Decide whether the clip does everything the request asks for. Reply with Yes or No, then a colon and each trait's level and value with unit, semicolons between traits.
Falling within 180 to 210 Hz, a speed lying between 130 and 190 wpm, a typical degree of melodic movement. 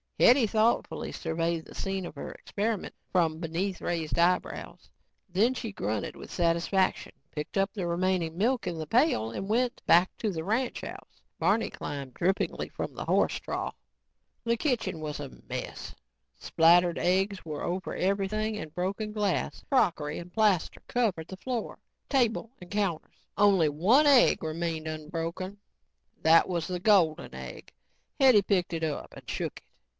Yes: medium, 185 Hz; average, 155 wpm; average, 4.5 semitones